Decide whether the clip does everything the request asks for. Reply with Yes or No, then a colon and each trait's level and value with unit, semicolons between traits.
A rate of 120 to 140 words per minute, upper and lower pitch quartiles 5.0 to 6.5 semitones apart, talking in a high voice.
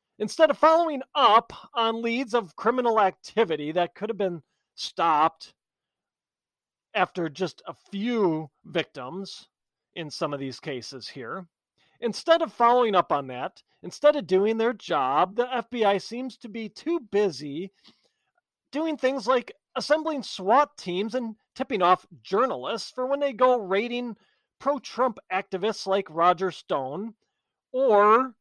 Yes: slow, 135 wpm; wide, 5.5 semitones; high, 220 Hz